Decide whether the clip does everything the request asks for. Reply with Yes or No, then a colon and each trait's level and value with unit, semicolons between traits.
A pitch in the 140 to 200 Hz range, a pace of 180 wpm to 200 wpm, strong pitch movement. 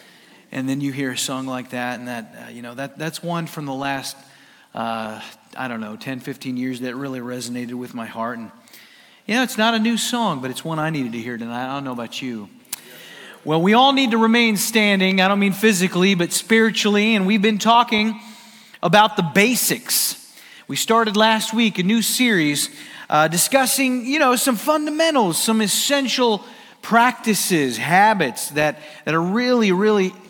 Yes: medium, 185 Hz; average, 190 wpm; wide, 8.9 semitones